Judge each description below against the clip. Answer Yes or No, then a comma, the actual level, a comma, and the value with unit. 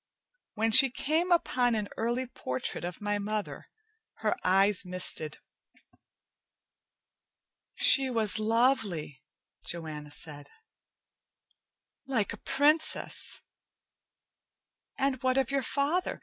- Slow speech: Yes, slow, 95 wpm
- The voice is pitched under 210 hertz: No, high, 225 Hz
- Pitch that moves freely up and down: Yes, wide, 6.6 semitones